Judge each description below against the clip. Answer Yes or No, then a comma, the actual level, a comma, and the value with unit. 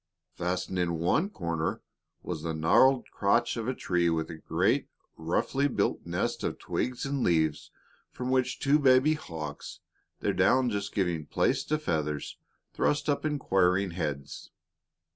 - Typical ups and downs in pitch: No, wide, 8.0 semitones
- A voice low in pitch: Yes, very low, 95 Hz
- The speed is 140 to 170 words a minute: Yes, average, 145 wpm